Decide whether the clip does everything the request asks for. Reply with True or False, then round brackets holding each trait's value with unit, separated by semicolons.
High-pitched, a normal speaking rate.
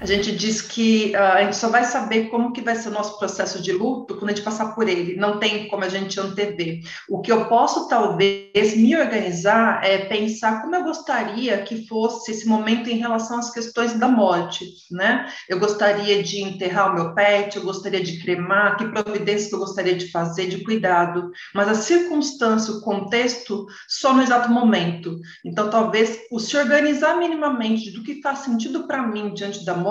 False (215 Hz; 195 wpm)